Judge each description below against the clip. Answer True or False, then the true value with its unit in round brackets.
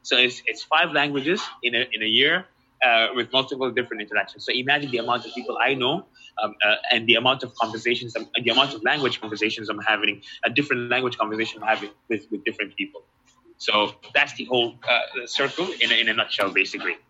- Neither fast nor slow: False (210 wpm)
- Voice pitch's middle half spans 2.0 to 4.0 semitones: True (2.9 semitones)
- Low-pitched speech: True (120 Hz)